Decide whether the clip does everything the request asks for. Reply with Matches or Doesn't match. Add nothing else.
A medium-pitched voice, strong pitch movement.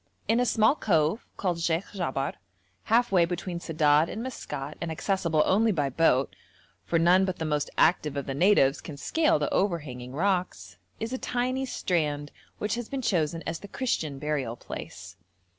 Matches